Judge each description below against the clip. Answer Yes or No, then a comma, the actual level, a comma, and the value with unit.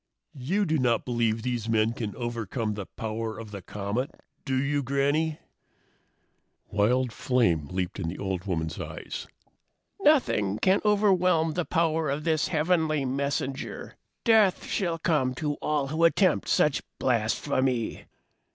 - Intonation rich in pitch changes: Yes, wide, 6.3 semitones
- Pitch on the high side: No, low, 130 Hz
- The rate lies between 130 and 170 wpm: Yes, slow, 135 wpm